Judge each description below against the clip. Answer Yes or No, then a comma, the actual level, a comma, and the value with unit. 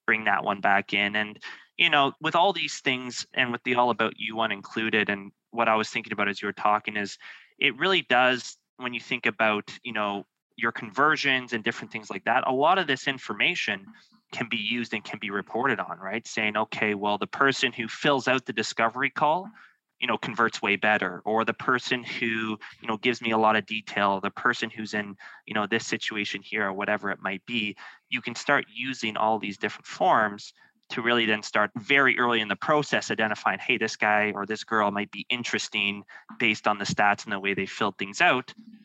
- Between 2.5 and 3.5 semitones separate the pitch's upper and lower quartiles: Yes, average, 2.9 semitones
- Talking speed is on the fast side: Yes, fast, 220 wpm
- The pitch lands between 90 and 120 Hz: Yes, low, 110 Hz